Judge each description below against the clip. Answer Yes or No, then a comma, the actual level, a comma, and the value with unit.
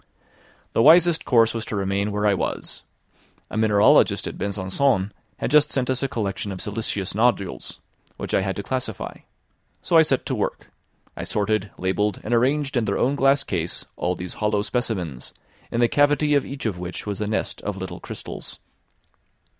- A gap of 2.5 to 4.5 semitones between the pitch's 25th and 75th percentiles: No, average, 5.0 semitones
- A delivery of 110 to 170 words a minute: No, average, 180 wpm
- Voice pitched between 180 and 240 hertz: No, low, 110 Hz